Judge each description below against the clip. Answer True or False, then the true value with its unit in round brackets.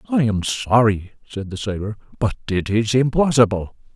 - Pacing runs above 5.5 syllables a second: False (4.9 syllables/s)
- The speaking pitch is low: True (110 Hz)